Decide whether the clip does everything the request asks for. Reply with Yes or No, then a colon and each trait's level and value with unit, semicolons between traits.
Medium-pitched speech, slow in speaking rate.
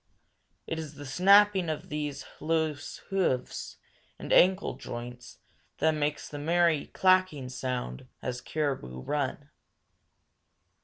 Yes: medium, 150 Hz; slow, 110 wpm